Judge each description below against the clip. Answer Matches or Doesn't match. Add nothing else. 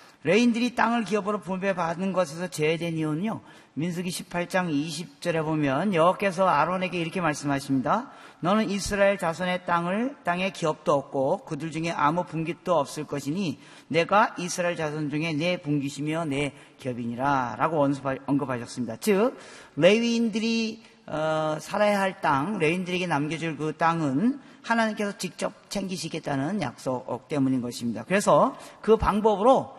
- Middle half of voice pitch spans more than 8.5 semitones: Doesn't match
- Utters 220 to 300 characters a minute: Doesn't match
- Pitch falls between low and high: Matches